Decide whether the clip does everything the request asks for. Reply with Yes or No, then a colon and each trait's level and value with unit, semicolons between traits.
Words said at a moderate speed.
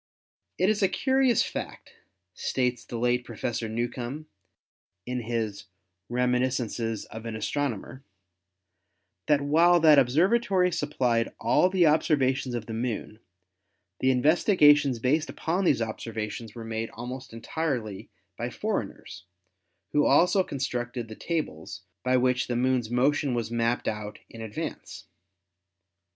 No: slow, 125 wpm